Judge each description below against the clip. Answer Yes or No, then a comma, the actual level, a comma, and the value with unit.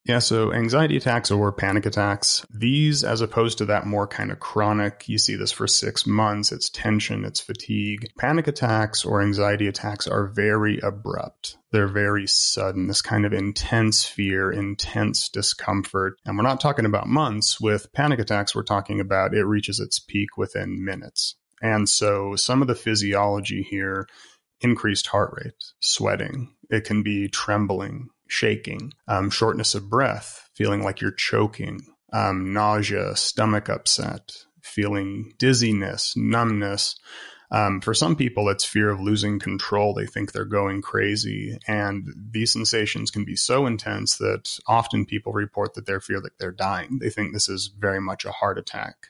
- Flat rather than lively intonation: Yes, narrow, 2.1 semitones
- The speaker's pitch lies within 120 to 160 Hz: No, low, 105 Hz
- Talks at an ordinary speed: Yes, average, 165 wpm